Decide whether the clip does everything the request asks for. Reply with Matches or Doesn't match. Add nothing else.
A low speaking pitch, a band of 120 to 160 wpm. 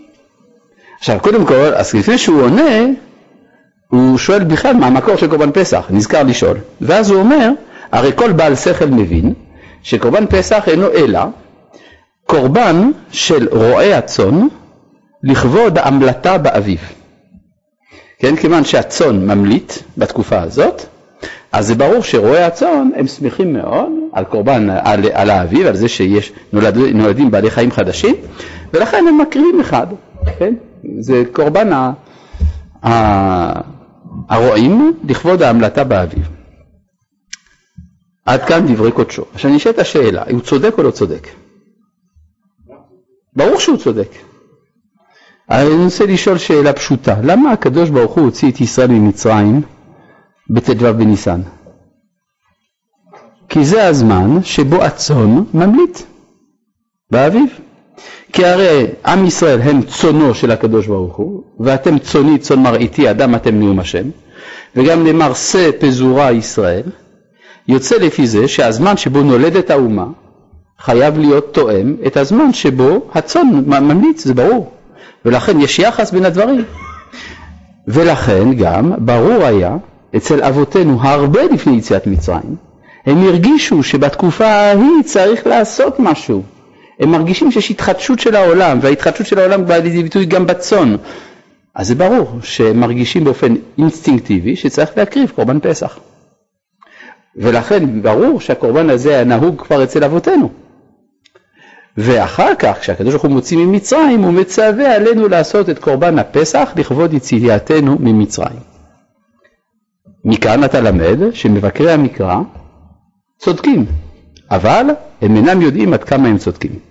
Doesn't match